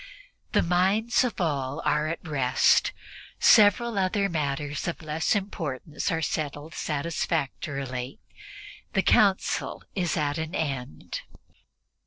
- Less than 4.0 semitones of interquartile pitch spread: No, average, 4.7 semitones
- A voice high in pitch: No, medium, 160 Hz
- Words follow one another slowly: Yes, slow, 110 wpm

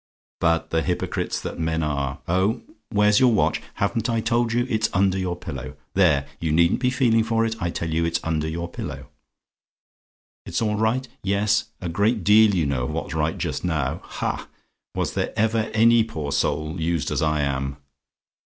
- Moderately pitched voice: No, very low, 90 Hz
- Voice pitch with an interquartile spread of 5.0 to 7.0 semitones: Yes, wide, 5.6 semitones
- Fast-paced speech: No, average, 190 wpm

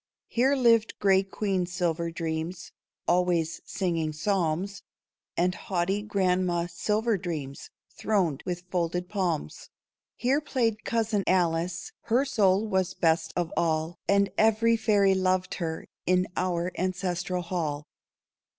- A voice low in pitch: No, medium, 185 Hz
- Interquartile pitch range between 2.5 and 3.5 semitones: Yes, average, 3.1 semitones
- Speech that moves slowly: Yes, slow, 120 wpm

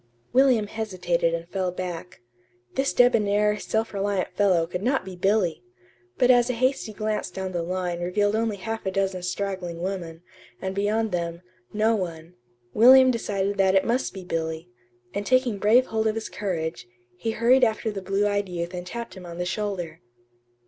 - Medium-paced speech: Yes, average, 175 wpm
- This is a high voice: Yes, high, 195 Hz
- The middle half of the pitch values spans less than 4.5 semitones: Yes, average, 3.7 semitones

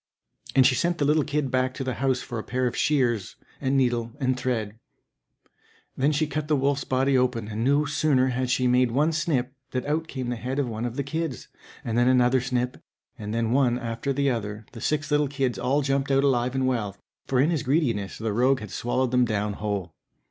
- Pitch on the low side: Yes, low, 130 Hz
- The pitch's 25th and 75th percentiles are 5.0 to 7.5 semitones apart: No, average, 2.7 semitones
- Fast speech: Yes, fast, 220 wpm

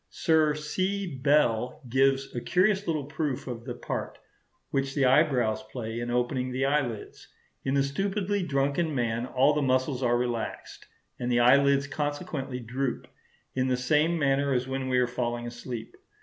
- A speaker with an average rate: Yes, average, 165 wpm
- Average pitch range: Yes, average, 3.2 semitones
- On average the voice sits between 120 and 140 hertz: Yes, low, 135 Hz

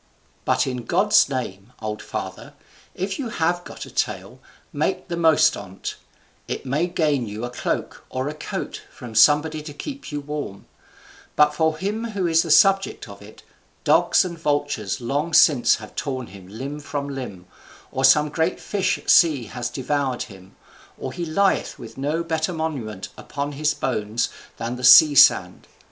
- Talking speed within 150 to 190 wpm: Yes, average, 170 wpm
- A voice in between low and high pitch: Yes, medium, 145 Hz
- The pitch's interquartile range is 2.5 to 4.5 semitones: No, average, 4.9 semitones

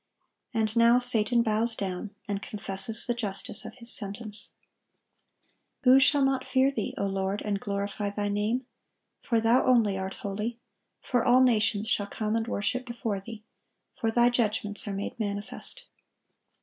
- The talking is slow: No, average, 155 wpm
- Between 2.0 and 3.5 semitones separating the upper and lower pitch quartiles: Yes, average, 2.8 semitones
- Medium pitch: No, high, 220 Hz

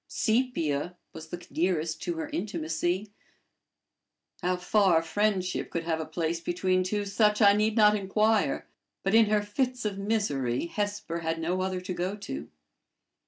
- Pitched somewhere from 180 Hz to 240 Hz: Yes, medium, 185 Hz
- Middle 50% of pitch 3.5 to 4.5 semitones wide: Yes, average, 4.0 semitones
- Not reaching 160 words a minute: Yes, average, 150 wpm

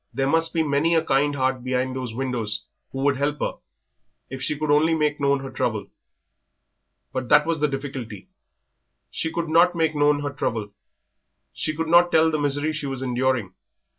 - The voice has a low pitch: No, medium, 145 Hz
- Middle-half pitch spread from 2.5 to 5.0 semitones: Yes, average, 3.1 semitones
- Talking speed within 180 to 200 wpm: Yes, average, 185 wpm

